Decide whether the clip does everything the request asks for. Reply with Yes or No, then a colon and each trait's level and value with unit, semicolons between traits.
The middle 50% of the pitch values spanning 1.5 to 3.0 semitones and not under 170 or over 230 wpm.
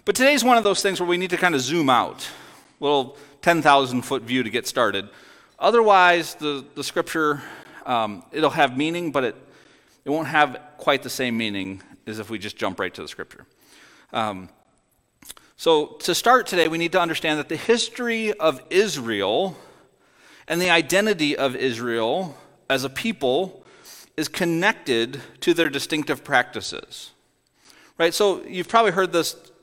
No: average, 5.2 semitones; average, 175 wpm